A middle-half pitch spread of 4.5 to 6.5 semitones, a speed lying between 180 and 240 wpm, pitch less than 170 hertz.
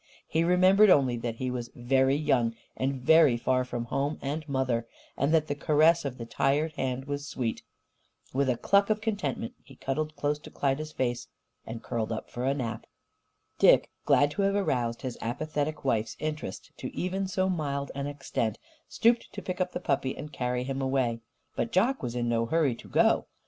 No: average, 4.1 semitones; average, 190 wpm; medium, 140 Hz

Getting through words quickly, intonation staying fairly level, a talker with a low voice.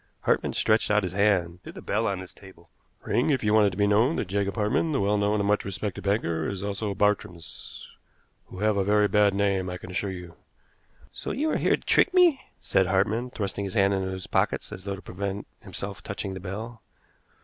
Yes: fast, 225 wpm; narrow, 1.9 semitones; low, 100 Hz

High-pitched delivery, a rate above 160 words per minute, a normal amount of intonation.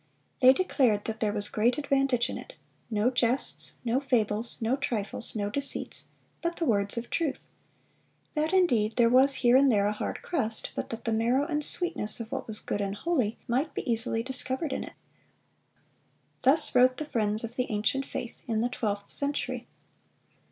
Yes: high, 240 Hz; average, 180 wpm; average, 3.9 semitones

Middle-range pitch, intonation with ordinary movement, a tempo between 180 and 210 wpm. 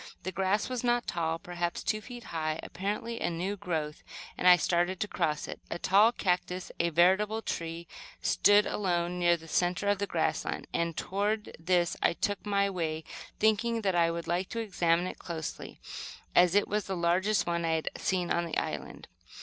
Yes: medium, 180 Hz; average, 3.2 semitones; average, 190 wpm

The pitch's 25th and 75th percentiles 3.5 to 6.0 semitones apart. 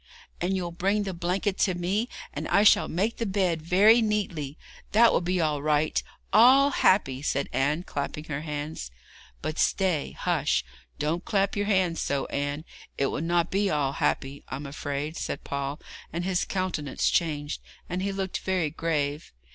Yes: average, 4.6 semitones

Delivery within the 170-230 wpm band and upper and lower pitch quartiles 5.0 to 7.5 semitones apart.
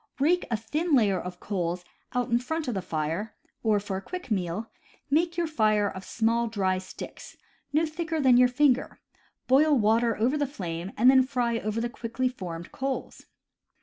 Yes: average, 190 wpm; average, 5.3 semitones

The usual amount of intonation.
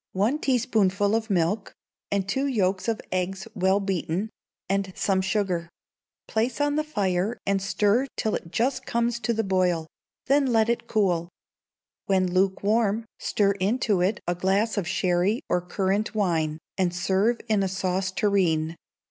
Yes: average, 3.1 semitones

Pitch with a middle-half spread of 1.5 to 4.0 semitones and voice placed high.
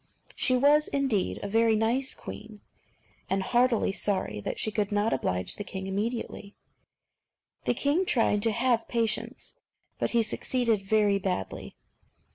Yes: average, 3.4 semitones; high, 220 Hz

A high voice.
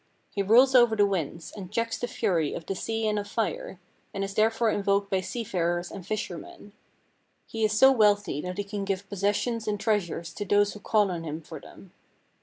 Yes: high, 205 Hz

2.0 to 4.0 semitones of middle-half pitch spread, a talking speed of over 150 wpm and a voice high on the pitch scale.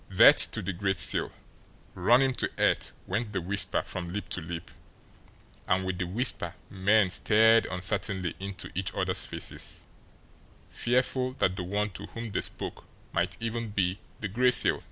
No: average, 3.5 semitones; average, 165 wpm; low, 100 Hz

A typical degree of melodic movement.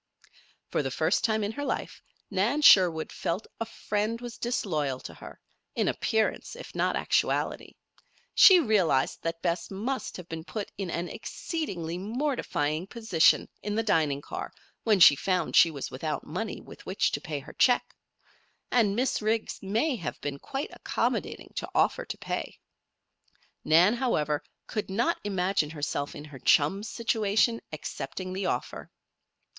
No: wide, 5.8 semitones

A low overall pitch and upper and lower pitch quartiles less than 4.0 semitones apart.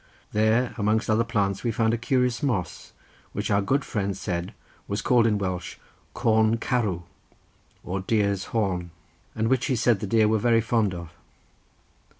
Yes: low, 110 Hz; average, 2.8 semitones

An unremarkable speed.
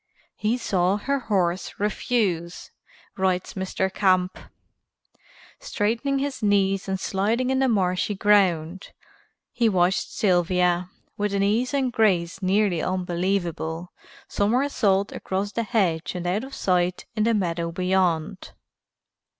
No: slow, 120 wpm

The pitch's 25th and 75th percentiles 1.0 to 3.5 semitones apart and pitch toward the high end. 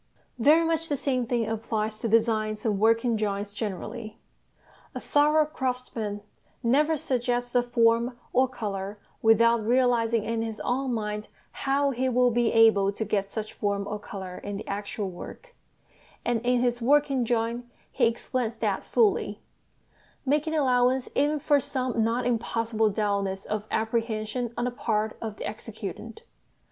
Yes: average, 2.7 semitones; high, 230 Hz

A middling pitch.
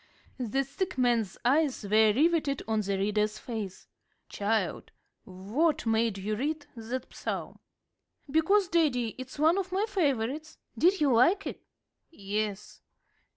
No: very high, 250 Hz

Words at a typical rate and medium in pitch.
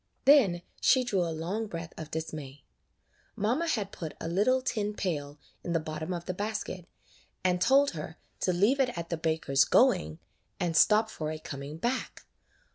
Yes: average, 175 wpm; medium, 175 Hz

